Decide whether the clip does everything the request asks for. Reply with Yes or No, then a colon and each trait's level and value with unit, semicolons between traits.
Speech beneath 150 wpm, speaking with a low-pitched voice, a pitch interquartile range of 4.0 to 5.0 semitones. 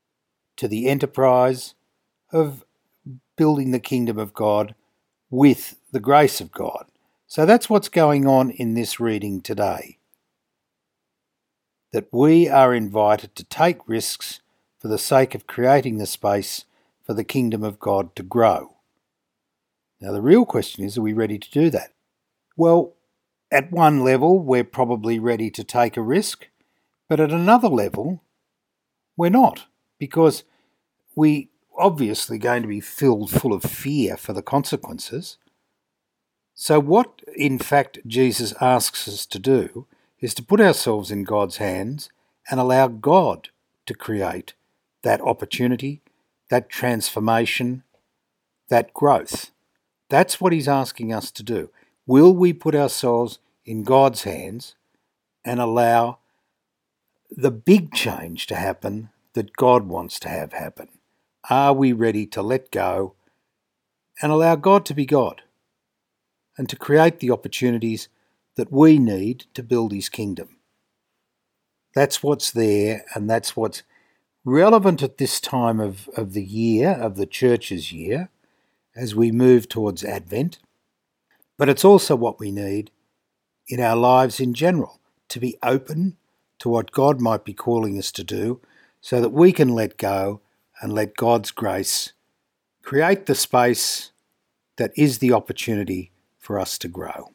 Yes: average, 140 wpm; low, 125 Hz; average, 4.5 semitones